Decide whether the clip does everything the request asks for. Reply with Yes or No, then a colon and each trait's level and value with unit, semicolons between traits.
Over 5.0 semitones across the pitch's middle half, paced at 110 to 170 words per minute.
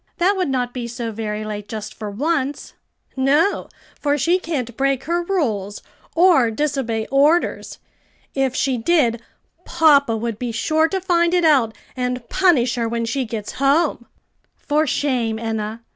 Yes: wide, 5.5 semitones; average, 155 wpm